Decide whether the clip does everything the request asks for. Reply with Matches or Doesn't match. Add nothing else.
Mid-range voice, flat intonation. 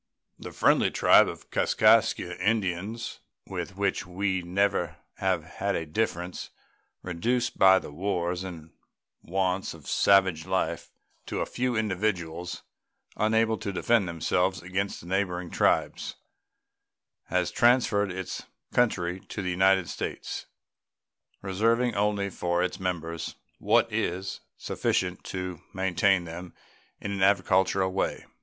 Doesn't match